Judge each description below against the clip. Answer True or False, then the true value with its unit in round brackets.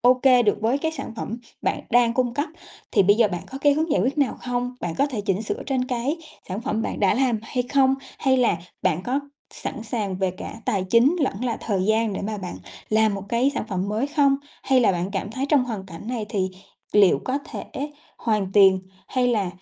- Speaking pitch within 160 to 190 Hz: False (230 Hz)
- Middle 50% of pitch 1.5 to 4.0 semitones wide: False (4.6 semitones)